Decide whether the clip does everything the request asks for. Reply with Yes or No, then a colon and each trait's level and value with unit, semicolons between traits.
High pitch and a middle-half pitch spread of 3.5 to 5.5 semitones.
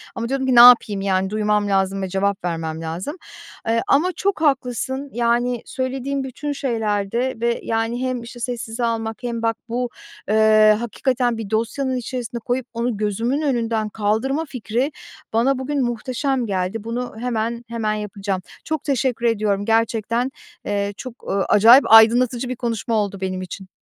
No: high, 230 Hz; average, 3.1 semitones